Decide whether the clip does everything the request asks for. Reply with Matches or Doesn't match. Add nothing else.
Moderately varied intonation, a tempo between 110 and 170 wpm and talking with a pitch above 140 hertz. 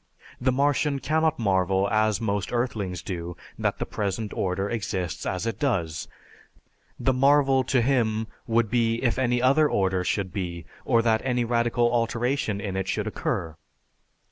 Doesn't match